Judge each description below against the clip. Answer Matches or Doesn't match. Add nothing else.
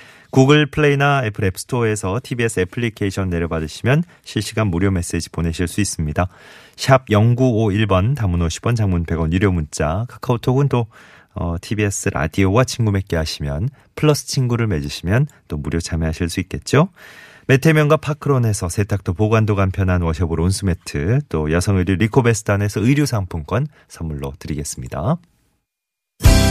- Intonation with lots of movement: Matches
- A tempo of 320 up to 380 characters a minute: Matches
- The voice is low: Matches